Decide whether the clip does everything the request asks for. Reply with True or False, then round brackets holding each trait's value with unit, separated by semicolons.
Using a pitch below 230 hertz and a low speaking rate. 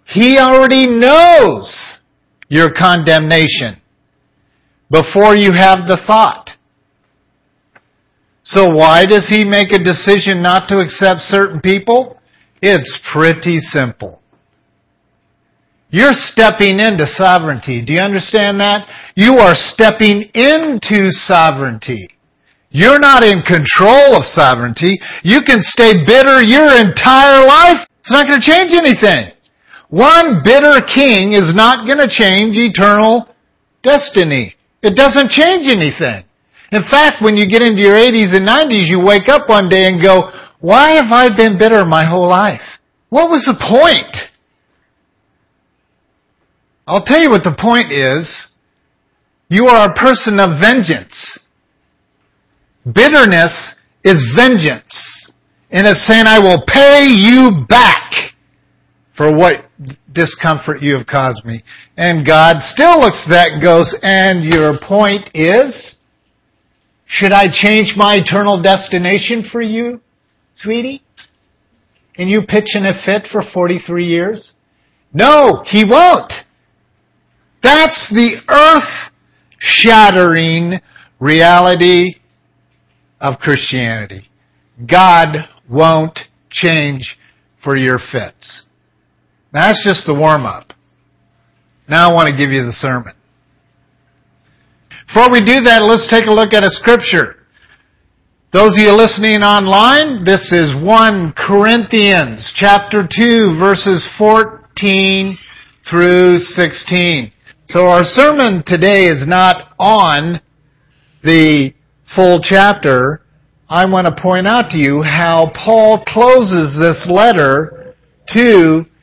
True (190 Hz; 120 wpm)